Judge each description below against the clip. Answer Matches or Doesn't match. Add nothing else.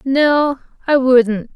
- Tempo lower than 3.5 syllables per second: Matches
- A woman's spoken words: Matches